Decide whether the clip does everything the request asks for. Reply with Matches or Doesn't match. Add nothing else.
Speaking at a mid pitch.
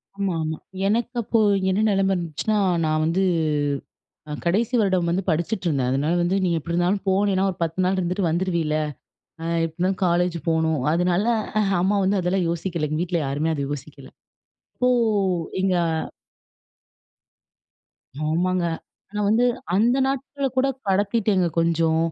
Matches